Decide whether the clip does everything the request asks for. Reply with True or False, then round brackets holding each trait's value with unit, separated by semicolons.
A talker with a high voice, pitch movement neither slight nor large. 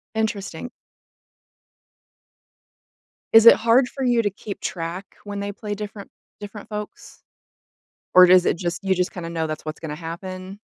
True (195 Hz; 3.3 semitones)